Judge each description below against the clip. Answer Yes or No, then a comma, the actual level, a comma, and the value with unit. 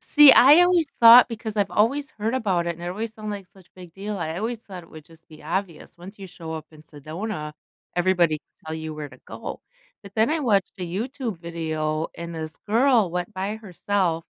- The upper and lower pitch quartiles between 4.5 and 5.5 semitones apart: Yes, average, 5.0 semitones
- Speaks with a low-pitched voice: No, medium, 185 Hz